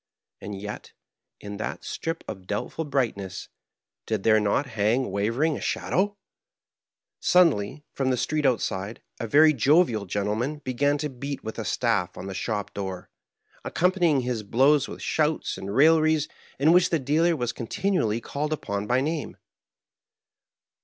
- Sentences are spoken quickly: No, average, 155 wpm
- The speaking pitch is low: Yes, low, 130 Hz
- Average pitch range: No, wide, 6.5 semitones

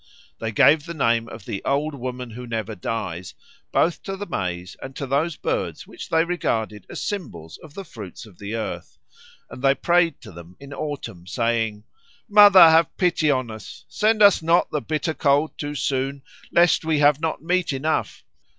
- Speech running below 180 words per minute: No, average, 185 wpm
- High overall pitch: No, medium, 140 Hz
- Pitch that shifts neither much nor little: No, wide, 6.3 semitones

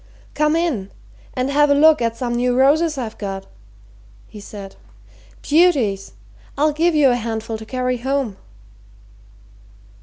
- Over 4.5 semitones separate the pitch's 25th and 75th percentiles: Yes, average, 4.9 semitones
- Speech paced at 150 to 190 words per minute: No, average, 140 wpm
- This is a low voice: No, very high, 255 Hz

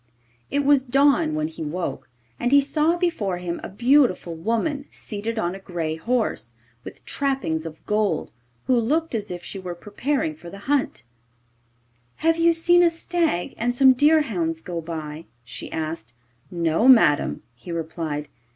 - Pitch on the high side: Yes, high, 205 Hz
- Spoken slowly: No, average, 160 wpm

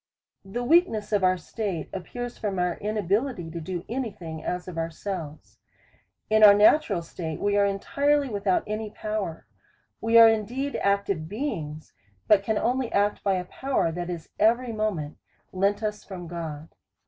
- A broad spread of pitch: No, average, 4.0 semitones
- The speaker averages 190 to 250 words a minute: No, average, 170 wpm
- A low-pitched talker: No, high, 200 Hz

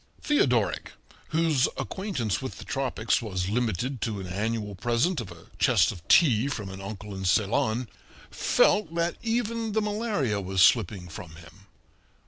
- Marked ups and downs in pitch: Yes, wide, 8.4 semitones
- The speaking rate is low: No, average, 150 wpm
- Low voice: Yes, low, 115 Hz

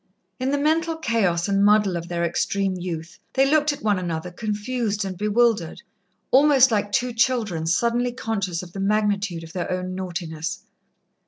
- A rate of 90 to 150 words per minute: No, average, 165 wpm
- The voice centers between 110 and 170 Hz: No, high, 205 Hz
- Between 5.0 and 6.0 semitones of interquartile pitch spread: Yes, average, 5.3 semitones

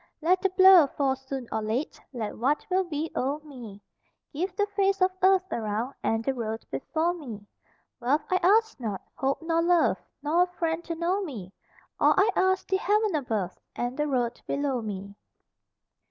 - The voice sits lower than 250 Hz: No, very high, 295 Hz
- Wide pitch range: Yes, wide, 7.3 semitones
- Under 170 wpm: No, average, 180 wpm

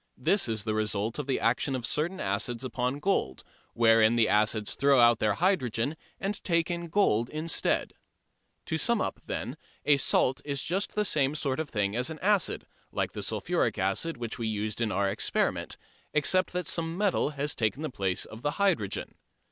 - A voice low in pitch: Yes, low, 130 Hz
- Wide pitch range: Yes, wide, 6.8 semitones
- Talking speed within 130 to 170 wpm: No, average, 190 wpm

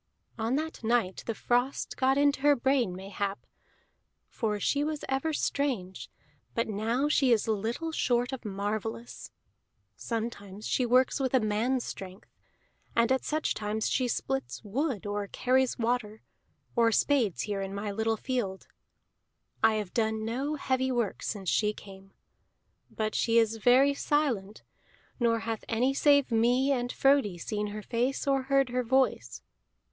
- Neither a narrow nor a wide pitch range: Yes, average, 3.9 semitones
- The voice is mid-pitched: No, high, 235 Hz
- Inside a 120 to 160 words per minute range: Yes, average, 150 wpm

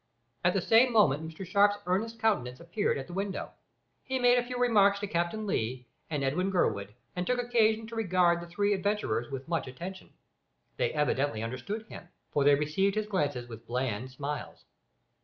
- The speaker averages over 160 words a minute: Yes, average, 180 wpm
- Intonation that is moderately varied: No, wide, 7.2 semitones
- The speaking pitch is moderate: Yes, medium, 180 Hz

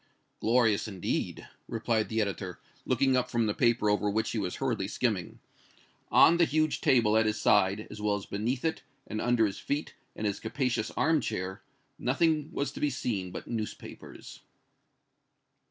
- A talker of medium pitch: No, low, 110 Hz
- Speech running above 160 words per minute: Yes, average, 170 wpm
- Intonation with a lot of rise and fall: No, average, 3.6 semitones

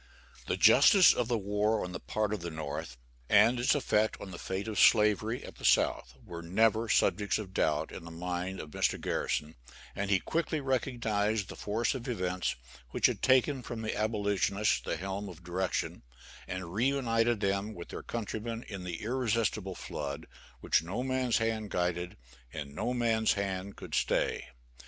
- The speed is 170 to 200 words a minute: Yes, average, 175 wpm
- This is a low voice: Yes, low, 105 Hz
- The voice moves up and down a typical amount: Yes, average, 3.9 semitones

